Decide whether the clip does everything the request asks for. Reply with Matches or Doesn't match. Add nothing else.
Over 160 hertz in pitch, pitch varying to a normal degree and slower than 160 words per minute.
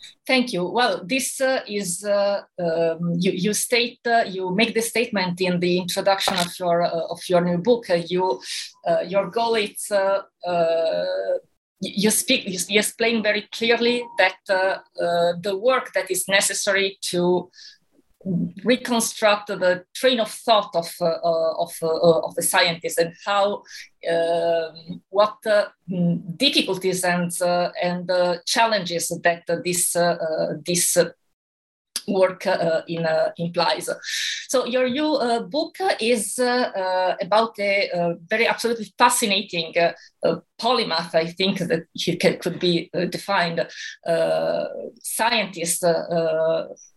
Matches